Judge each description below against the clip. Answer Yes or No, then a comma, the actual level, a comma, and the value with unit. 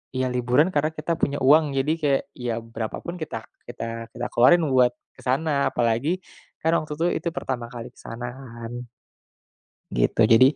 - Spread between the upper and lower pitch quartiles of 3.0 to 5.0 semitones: Yes, average, 4.1 semitones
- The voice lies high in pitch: No, low, 130 Hz